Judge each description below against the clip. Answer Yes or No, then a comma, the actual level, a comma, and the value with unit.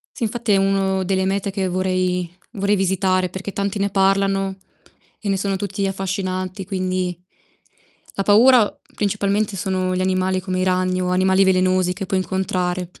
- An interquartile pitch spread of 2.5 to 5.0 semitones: No, narrow, 1.1 semitones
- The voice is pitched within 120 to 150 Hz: No, high, 190 Hz